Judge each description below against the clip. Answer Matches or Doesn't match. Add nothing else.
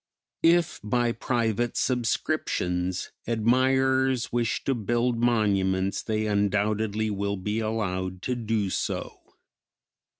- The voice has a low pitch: Matches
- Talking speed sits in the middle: Doesn't match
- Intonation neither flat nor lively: Matches